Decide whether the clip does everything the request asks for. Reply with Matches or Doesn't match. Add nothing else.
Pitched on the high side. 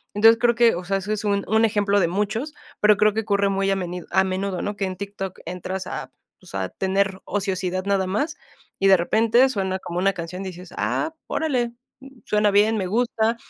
Matches